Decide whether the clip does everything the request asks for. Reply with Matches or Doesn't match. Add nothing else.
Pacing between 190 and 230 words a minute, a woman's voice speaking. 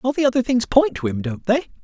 Doesn't match